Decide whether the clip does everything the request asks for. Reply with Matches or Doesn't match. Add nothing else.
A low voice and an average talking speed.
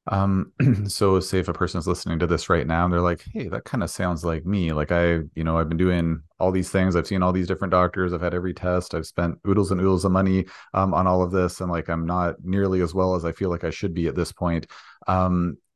Doesn't match